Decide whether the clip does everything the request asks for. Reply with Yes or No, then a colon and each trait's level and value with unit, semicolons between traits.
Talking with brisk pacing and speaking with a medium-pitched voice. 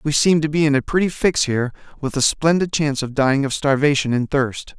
Yes: fast, 240 wpm; medium, 145 Hz